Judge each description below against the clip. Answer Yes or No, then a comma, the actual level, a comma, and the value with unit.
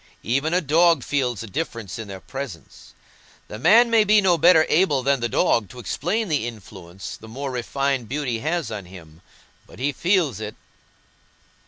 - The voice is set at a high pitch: No, low, 135 Hz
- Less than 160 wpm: No, average, 175 wpm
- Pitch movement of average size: No, wide, 6.7 semitones